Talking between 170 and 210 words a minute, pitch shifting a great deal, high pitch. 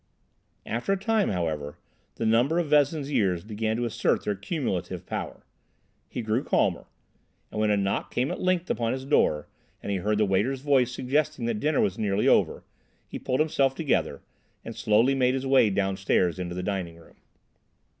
No: average, 180 wpm; wide, 5.7 semitones; low, 115 Hz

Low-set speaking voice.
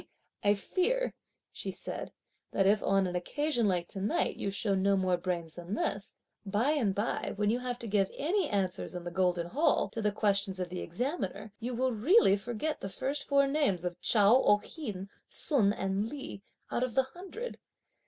No: high, 205 Hz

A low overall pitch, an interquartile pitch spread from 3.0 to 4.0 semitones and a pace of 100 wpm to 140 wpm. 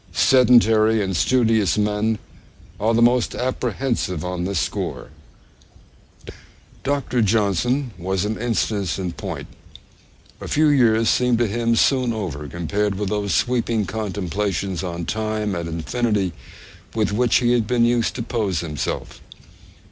Yes: low, 110 Hz; average, 3.7 semitones; slow, 135 wpm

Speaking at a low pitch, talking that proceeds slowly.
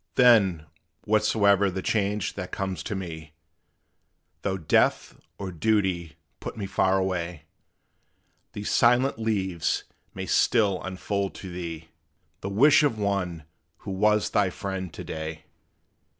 Yes: very low, 95 Hz; slow, 125 wpm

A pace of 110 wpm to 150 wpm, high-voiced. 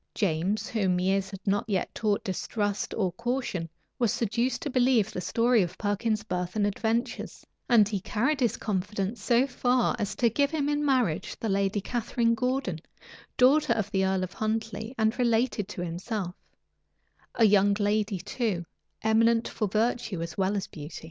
No: average, 170 wpm; high, 215 Hz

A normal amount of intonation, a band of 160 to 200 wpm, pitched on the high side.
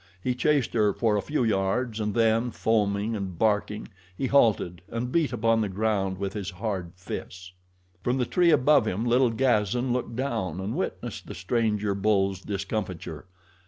No: average, 3.8 semitones; average, 165 wpm; low, 110 Hz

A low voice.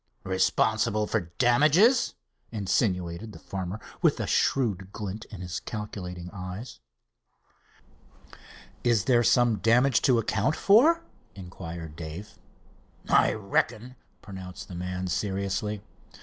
Yes: low, 105 Hz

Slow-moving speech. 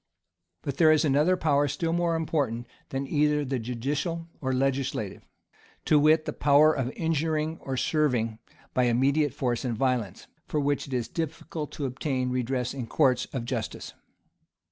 No: average, 160 wpm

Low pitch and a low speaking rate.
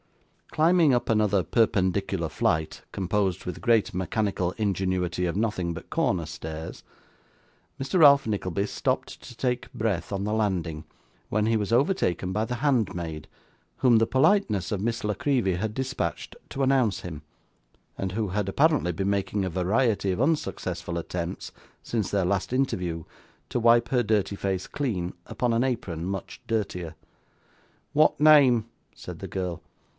No: low, 105 Hz; average, 150 wpm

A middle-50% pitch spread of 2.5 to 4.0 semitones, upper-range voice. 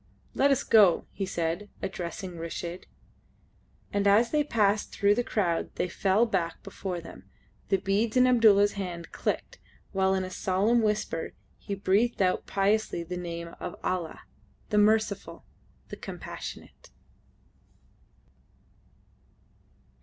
Yes: average, 3.1 semitones; high, 195 Hz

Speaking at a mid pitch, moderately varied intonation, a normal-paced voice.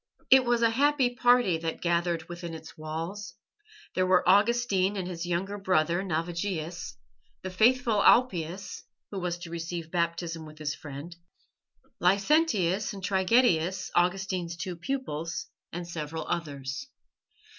No: medium, 180 Hz; average, 3.4 semitones; slow, 130 wpm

